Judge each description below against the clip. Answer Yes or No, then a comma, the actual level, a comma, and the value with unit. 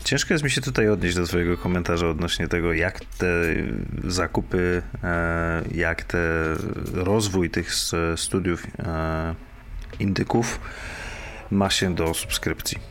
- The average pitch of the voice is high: No, very low, 90 Hz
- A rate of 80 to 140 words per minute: Yes, slow, 110 wpm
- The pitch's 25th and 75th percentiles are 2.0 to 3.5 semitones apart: No, average, 4.0 semitones